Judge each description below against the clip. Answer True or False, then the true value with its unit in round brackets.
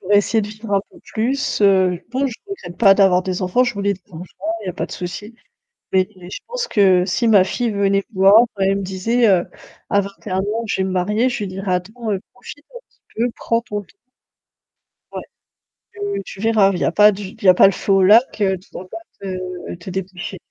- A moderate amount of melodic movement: True (3.2 semitones)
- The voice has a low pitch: False (200 Hz)